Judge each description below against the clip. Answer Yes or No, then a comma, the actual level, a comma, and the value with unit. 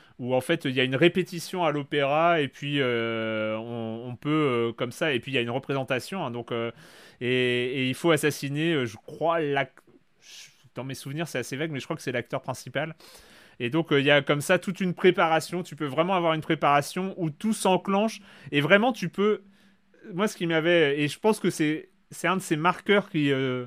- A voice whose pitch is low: No, medium, 150 Hz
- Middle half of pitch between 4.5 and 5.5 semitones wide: Yes, average, 5.1 semitones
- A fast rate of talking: Yes, fast, 230 wpm